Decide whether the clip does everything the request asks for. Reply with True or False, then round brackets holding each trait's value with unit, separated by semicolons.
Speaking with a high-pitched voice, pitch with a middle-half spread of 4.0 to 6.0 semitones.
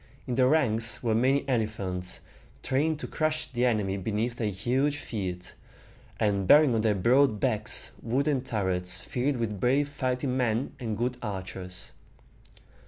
False (120 Hz; 4.3 semitones)